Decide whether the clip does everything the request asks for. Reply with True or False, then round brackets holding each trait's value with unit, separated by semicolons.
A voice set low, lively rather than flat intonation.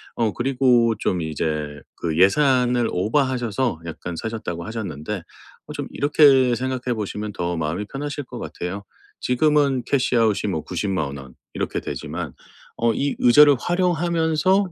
True (115 Hz; 7.3 semitones)